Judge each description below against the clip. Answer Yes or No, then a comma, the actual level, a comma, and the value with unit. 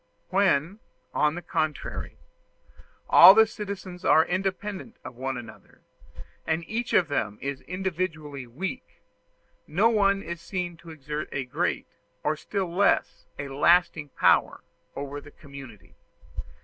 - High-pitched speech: No, medium, 170 Hz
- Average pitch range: Yes, average, 5.0 semitones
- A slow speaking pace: Yes, slow, 130 wpm